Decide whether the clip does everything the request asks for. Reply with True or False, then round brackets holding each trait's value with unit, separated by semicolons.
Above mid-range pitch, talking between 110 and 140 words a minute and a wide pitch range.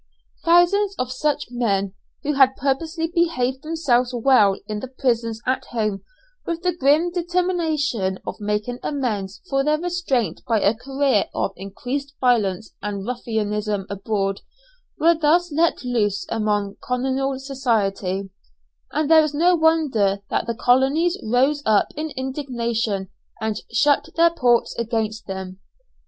True (250 Hz; 135 wpm; 6.1 semitones)